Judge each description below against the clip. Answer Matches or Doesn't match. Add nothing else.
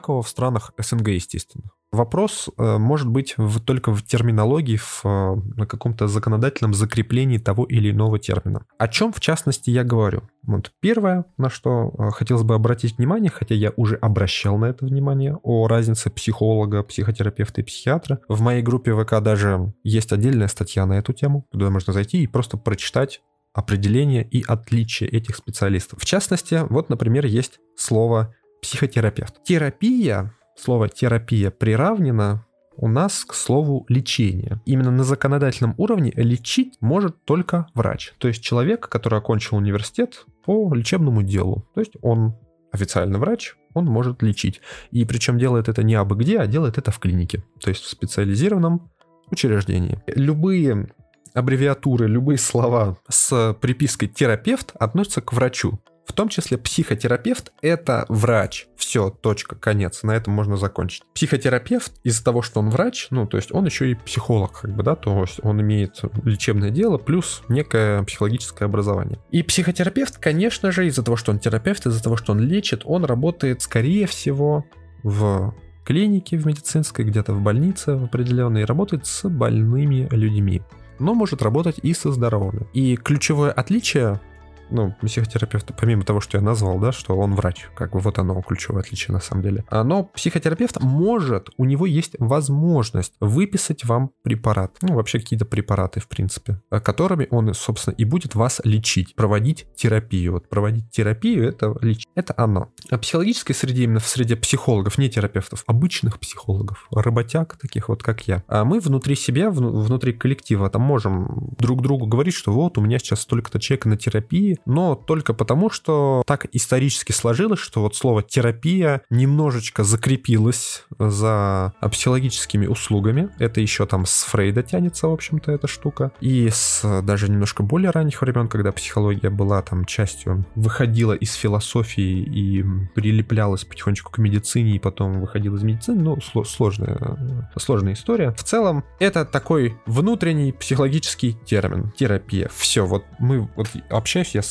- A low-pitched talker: Matches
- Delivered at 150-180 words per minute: Matches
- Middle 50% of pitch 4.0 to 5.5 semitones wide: Matches